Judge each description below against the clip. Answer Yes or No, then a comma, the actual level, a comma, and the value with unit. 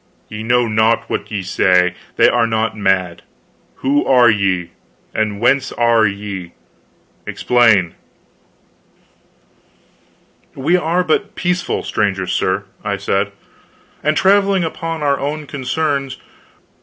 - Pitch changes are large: Yes, wide, 6.6 semitones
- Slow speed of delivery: Yes, slow, 115 wpm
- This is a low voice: Yes, low, 115 Hz